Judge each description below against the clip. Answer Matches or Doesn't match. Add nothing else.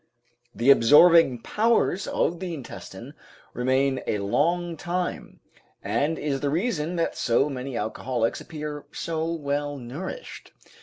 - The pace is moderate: Doesn't match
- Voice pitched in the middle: Matches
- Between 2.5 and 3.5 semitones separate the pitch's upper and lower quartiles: Doesn't match